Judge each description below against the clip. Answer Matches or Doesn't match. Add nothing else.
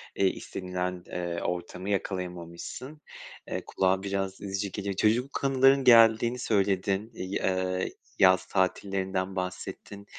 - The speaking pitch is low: Matches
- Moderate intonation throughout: Doesn't match